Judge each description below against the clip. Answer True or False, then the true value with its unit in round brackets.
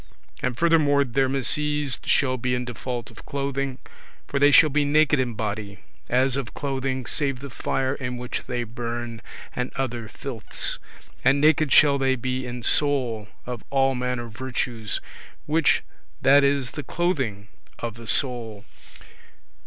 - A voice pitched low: True (130 Hz)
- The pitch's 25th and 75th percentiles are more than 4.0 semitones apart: False (2.7 semitones)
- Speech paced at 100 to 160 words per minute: True (150 wpm)